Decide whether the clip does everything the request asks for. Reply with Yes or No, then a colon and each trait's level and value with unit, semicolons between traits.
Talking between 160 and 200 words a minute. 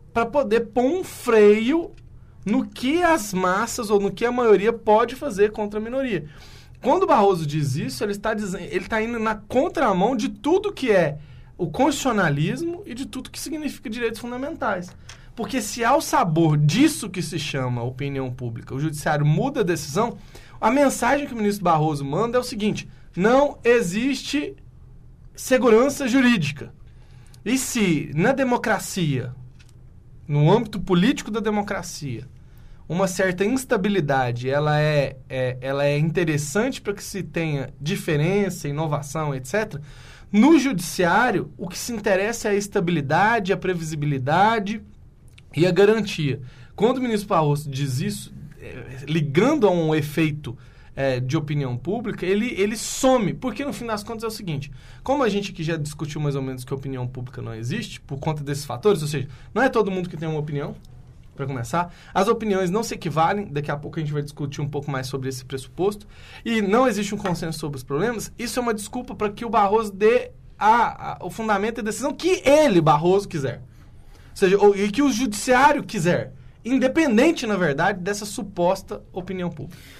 Yes: average, 175 wpm